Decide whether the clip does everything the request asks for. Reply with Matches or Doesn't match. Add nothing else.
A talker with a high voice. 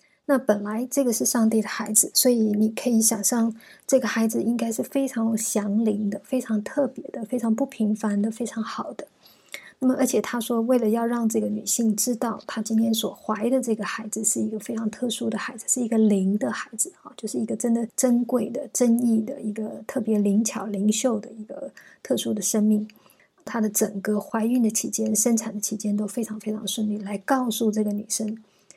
Matches